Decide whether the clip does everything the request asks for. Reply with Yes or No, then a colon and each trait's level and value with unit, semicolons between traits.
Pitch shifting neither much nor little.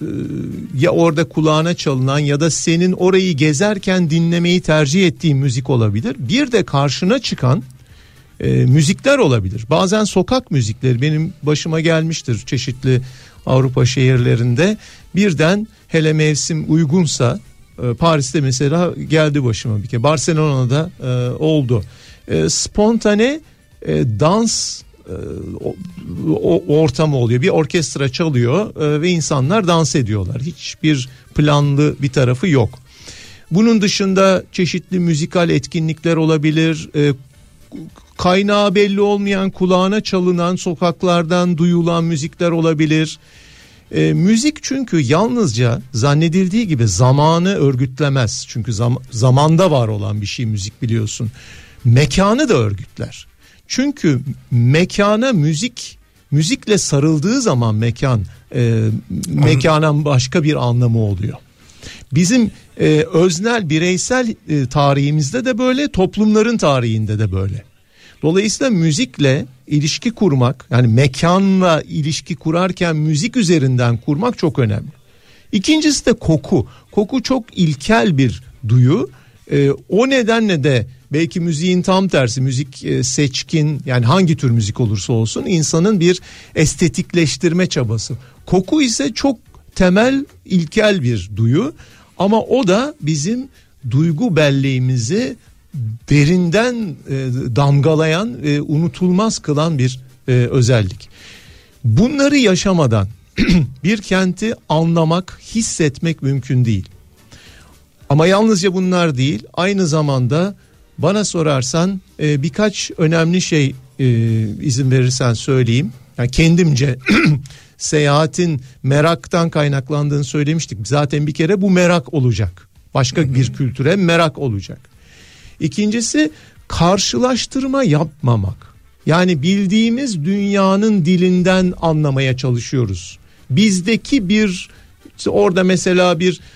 No: wide, 6.2 semitones